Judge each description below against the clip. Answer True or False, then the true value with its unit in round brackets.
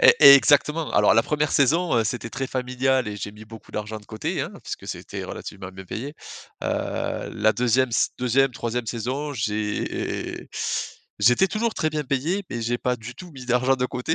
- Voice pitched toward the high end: False (125 Hz)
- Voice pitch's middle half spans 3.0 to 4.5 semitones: True (4.0 semitones)